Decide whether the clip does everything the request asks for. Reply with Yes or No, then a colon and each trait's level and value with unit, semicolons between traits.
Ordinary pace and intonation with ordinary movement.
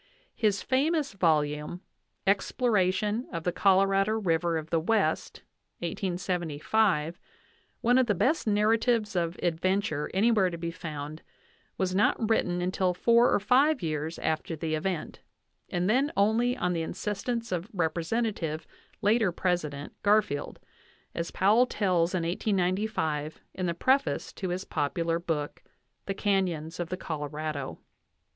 No: slow, 130 wpm; average, 4.5 semitones